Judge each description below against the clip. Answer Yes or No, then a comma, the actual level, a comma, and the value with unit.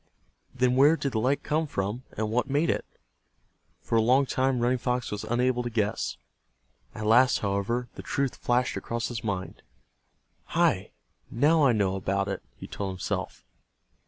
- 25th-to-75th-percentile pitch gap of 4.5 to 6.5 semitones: No, average, 3.3 semitones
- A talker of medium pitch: No, low, 120 Hz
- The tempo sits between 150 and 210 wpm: Yes, average, 165 wpm